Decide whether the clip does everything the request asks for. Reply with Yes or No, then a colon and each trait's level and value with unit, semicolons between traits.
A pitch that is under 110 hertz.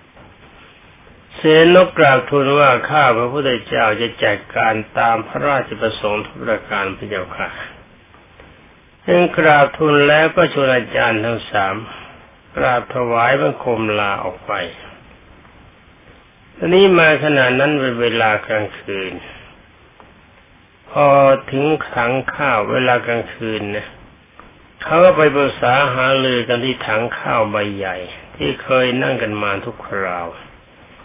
No: low, 120 Hz